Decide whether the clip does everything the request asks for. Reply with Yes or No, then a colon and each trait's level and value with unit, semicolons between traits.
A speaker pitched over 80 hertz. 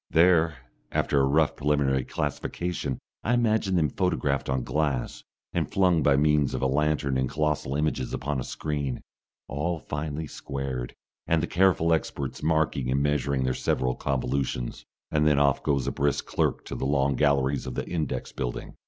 No: very low, 70 Hz